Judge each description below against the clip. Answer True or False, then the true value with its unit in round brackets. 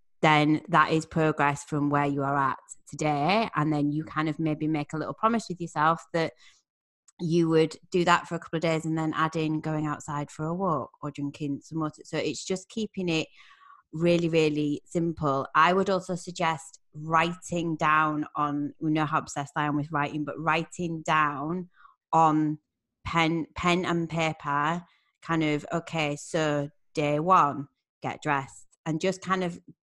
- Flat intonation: True (2.2 semitones)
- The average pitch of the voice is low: False (155 Hz)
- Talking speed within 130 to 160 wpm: False (175 wpm)